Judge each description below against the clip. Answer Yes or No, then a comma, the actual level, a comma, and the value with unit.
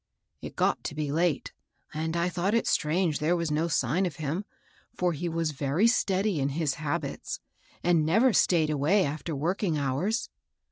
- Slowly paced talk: No, average, 175 wpm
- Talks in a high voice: No, medium, 165 Hz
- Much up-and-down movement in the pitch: No, average, 3.2 semitones